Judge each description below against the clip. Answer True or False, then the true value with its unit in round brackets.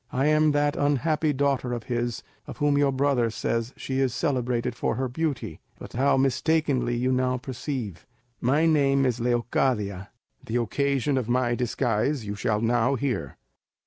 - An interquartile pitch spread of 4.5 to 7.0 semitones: False (2.9 semitones)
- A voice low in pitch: True (130 Hz)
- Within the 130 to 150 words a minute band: False (165 wpm)